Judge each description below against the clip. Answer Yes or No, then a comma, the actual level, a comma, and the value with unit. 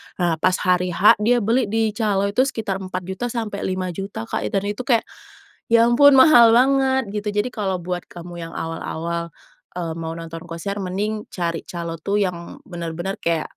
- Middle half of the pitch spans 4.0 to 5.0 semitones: Yes, average, 4.6 semitones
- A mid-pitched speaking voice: No, high, 195 Hz